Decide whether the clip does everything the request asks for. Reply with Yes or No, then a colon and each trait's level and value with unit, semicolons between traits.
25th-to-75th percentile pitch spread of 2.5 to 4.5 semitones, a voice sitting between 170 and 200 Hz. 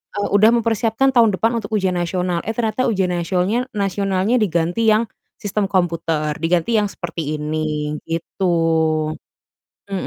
Yes: average, 3.9 semitones; high, 190 Hz